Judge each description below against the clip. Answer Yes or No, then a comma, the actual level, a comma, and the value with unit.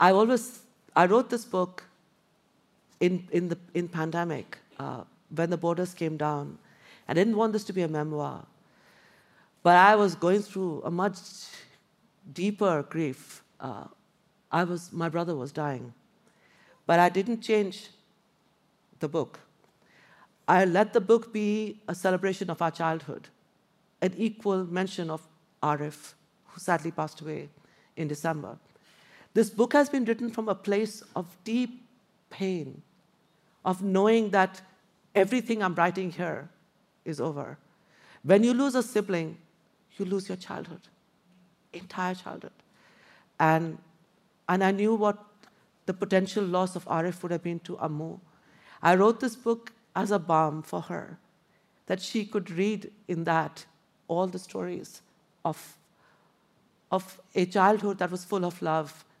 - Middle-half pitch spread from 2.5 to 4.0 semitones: Yes, average, 3.7 semitones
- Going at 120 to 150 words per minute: Yes, average, 145 wpm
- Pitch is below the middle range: No, medium, 185 Hz